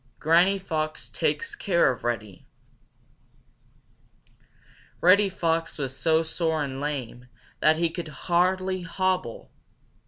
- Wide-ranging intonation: No, average, 4.0 semitones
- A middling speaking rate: No, slow, 105 wpm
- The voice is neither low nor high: Yes, medium, 165 Hz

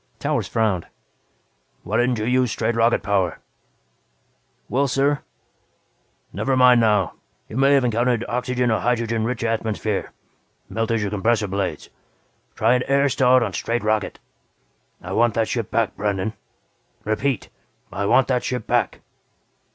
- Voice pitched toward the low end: Yes, low, 115 Hz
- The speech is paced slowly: No, average, 145 wpm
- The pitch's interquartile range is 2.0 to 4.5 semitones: Yes, average, 2.7 semitones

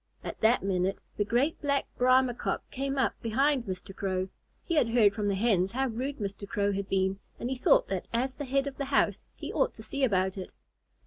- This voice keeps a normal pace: No, fast, 220 wpm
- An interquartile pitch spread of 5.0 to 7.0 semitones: Yes, average, 5.3 semitones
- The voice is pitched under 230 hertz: No, high, 235 Hz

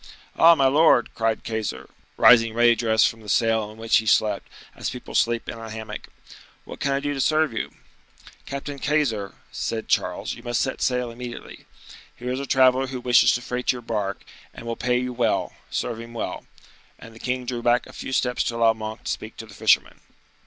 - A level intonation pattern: Yes, narrow, 2.2 semitones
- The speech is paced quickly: Yes, fast, 210 wpm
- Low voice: Yes, low, 120 Hz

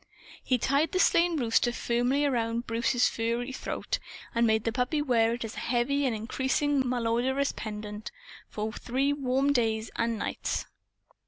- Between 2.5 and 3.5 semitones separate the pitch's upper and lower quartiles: Yes, average, 3.1 semitones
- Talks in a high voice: Yes, high, 245 Hz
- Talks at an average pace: Yes, average, 155 wpm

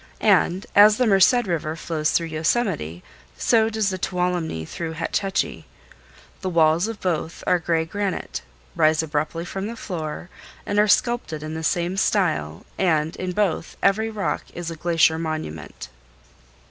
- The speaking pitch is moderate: Yes, medium, 170 Hz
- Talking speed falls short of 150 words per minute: No, average, 155 wpm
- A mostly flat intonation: No, average, 3.8 semitones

